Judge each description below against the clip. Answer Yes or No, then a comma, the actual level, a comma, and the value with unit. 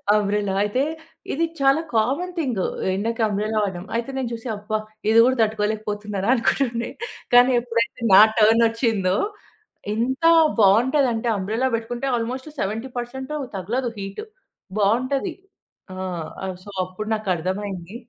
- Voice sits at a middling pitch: No, high, 225 Hz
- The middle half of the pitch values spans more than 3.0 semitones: Yes, average, 3.4 semitones